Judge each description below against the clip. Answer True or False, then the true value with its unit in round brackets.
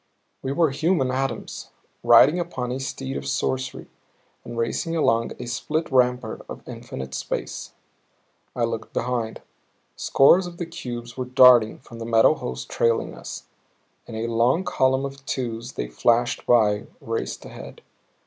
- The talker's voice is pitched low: True (125 Hz)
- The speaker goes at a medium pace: True (150 wpm)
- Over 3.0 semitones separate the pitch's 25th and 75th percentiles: False (2.7 semitones)